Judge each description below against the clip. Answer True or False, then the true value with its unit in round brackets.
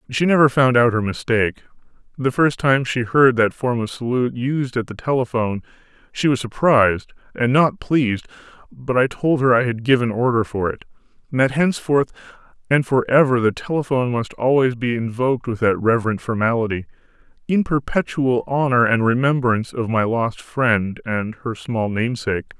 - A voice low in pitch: True (125 Hz)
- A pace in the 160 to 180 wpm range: True (165 wpm)